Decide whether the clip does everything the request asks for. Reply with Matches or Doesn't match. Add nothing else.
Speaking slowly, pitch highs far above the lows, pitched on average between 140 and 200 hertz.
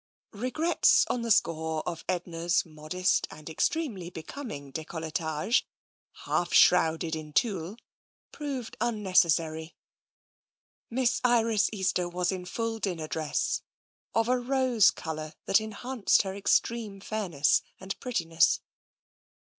Matches